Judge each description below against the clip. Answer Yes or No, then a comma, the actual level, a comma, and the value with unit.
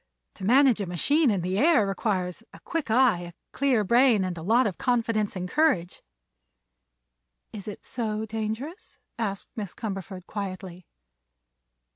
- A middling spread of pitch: Yes, average, 4.7 semitones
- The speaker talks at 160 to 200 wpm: No, average, 145 wpm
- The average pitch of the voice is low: No, high, 215 Hz